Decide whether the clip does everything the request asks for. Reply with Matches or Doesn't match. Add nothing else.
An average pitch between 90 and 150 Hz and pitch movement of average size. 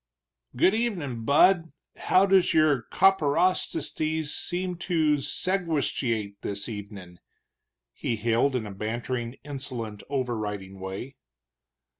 Doesn't match